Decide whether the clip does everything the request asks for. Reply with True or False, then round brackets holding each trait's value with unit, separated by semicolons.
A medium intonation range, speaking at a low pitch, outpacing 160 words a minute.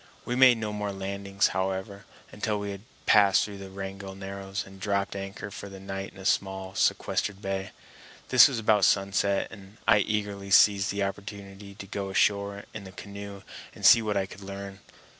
False (0.9 semitones; 100 Hz; 185 wpm)